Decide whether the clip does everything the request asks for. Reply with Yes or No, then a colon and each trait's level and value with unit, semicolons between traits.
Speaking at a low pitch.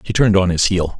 Yes: very low, 95 Hz